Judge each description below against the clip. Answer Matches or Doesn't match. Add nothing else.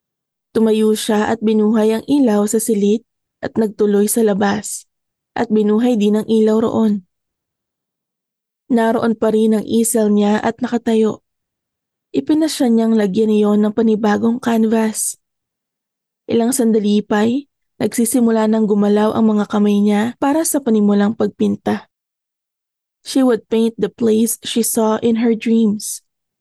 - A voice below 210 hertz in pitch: Doesn't match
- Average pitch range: Doesn't match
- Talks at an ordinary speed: Matches